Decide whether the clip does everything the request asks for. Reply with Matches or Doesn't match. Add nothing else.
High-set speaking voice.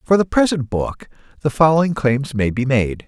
Doesn't match